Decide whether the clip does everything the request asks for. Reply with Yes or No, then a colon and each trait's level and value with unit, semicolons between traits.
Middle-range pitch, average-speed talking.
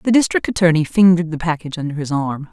No: medium, 165 Hz; fast, 215 wpm